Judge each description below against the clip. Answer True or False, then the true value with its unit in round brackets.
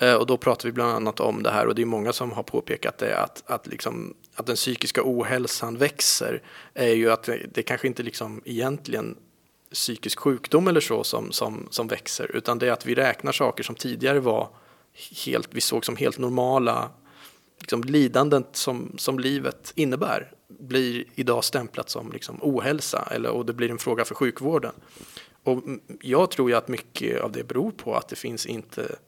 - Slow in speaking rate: False (190 wpm)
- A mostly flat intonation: True (2.1 semitones)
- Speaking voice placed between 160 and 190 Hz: False (125 Hz)